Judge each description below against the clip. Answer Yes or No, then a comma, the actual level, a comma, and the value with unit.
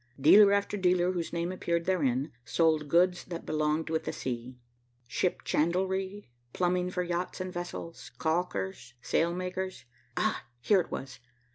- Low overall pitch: No, medium, 175 Hz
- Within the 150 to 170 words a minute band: No, average, 140 wpm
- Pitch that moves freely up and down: No, average, 3.1 semitones